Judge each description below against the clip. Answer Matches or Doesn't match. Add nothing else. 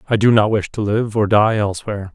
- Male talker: Matches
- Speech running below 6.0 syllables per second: Doesn't match